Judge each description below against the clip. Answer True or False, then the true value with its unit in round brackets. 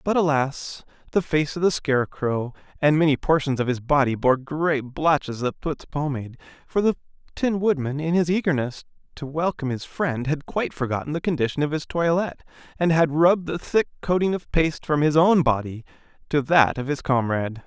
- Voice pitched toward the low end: False (150 Hz)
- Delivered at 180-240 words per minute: True (185 wpm)